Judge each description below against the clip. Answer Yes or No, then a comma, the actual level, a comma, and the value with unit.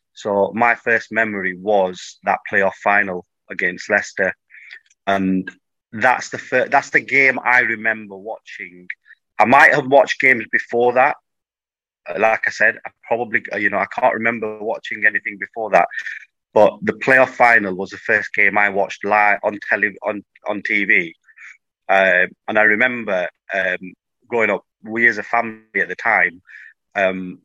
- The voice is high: No, low, 105 Hz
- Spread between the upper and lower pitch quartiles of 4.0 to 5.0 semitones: No, average, 2.9 semitones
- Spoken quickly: No, average, 155 wpm